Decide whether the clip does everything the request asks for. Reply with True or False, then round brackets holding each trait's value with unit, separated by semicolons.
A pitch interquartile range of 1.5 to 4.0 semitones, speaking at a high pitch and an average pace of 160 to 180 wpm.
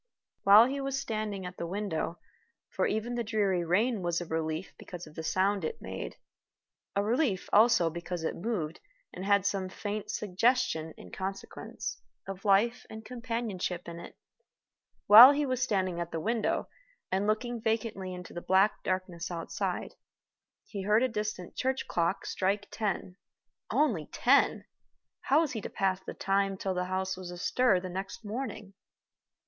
True (3.7 semitones; 195 Hz; 165 wpm)